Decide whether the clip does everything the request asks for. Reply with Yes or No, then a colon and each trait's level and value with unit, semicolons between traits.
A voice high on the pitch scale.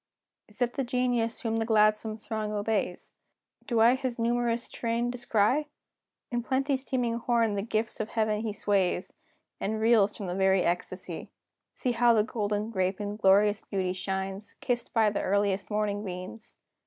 Yes: high, 220 Hz